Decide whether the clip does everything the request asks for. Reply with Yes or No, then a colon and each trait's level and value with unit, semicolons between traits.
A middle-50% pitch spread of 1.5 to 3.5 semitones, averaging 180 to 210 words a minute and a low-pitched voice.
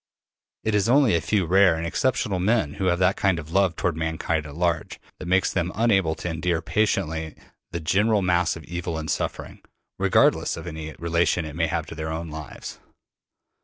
Yes: average, 3.1 semitones; average, 195 wpm; very low, 85 Hz